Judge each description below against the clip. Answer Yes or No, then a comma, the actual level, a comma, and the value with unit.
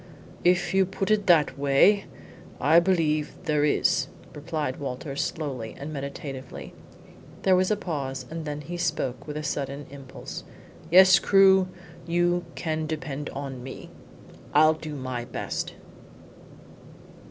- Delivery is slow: Yes, slow, 130 wpm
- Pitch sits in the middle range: Yes, medium, 150 Hz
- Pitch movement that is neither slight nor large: Yes, average, 4.0 semitones